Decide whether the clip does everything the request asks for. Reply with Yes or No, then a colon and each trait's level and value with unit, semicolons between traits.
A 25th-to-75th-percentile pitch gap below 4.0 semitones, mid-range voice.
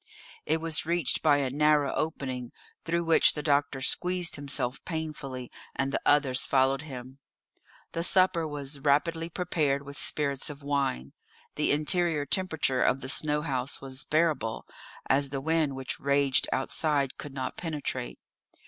Yes: average, 2.9 semitones; medium, 145 Hz